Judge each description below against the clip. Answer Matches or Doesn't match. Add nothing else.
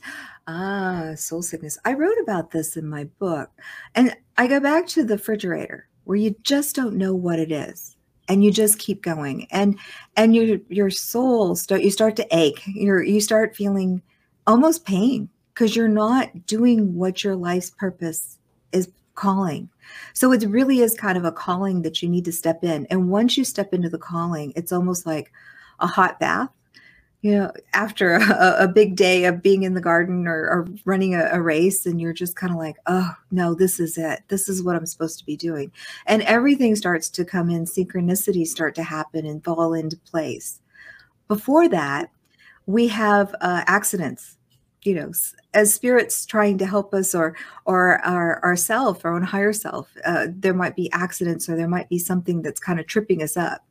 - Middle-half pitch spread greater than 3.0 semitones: Matches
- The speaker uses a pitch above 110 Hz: Matches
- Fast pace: Doesn't match